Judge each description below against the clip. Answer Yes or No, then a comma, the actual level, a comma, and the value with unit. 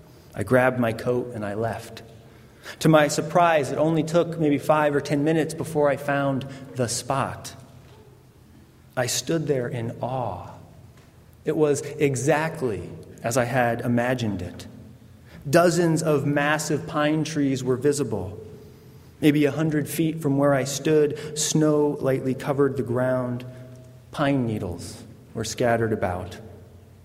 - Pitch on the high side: No, low, 135 Hz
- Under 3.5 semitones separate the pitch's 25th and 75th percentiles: No, average, 4.2 semitones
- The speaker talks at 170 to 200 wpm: No, slow, 135 wpm